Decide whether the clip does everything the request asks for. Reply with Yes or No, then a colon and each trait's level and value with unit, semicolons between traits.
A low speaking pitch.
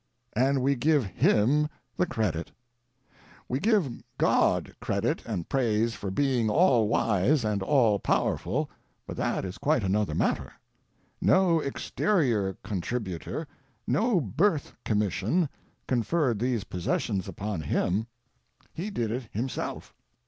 Yes: low, 120 Hz